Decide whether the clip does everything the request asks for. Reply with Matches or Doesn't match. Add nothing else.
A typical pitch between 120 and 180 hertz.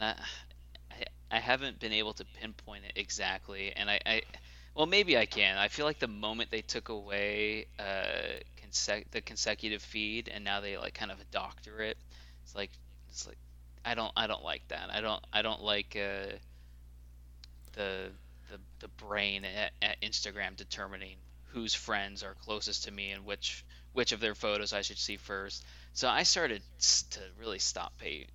Doesn't match